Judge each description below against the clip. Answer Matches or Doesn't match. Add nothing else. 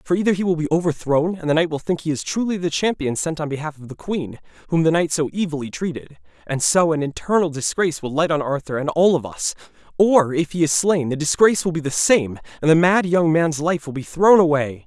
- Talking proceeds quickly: Matches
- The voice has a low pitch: Doesn't match